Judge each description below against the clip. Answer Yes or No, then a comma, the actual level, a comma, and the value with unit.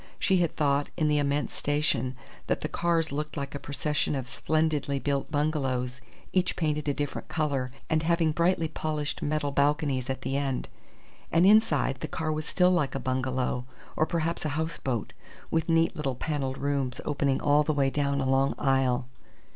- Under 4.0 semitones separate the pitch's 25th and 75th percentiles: Yes, narrow, 2.6 semitones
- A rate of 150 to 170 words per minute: No, average, 180 wpm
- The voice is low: No, medium, 145 Hz